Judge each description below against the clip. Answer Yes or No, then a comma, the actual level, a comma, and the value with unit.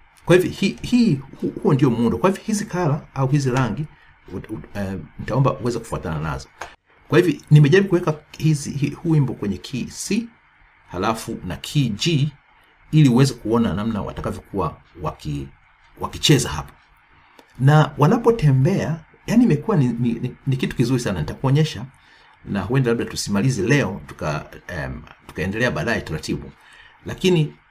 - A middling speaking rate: Yes, average, 130 wpm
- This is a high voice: No, medium, 140 Hz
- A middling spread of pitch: No, wide, 5.7 semitones